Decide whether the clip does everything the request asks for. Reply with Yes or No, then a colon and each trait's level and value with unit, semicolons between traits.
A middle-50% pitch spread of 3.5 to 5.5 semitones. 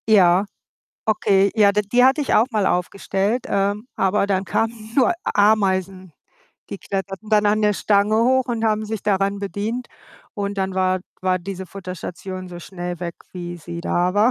No: narrow, 2.5 semitones